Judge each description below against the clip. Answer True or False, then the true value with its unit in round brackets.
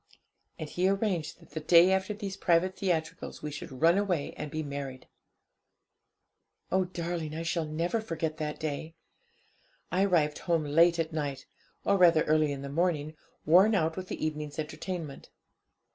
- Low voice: False (165 Hz)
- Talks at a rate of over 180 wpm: False (160 wpm)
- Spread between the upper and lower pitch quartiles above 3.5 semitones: False (3.0 semitones)